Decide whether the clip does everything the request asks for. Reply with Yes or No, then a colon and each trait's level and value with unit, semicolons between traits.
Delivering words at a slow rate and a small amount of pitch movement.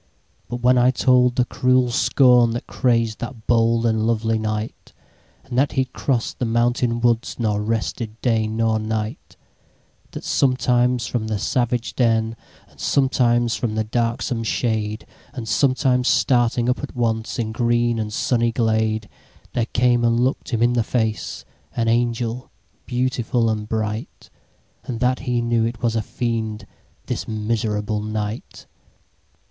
Yes: slow, 125 wpm; narrow, 1.8 semitones